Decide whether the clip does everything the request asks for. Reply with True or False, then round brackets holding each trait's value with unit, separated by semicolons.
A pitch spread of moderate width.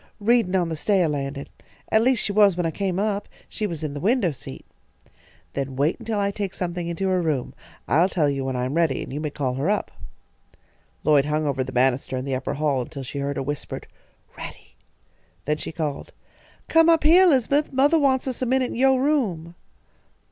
False (7.5 semitones)